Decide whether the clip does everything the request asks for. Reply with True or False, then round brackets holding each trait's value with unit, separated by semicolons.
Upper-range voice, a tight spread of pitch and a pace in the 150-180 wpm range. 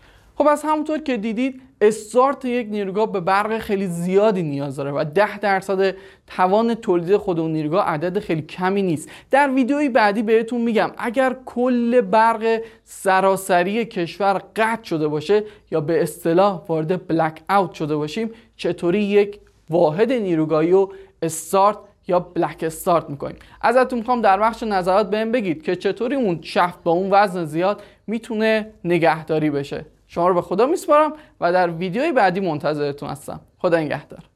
False (195 Hz; 4.6 semitones; 155 wpm)